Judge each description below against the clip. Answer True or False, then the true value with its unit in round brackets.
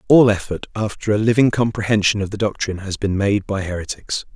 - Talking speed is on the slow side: False (195 wpm)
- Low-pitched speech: True (105 Hz)